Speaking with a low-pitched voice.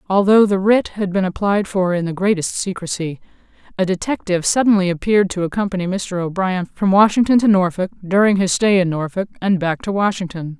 No: high, 190 Hz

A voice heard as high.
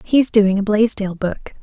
Yes: high, 210 Hz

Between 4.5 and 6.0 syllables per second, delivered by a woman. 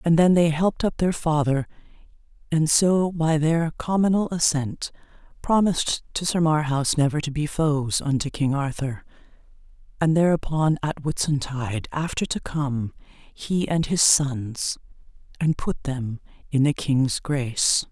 No: 4.2 syllables/s; female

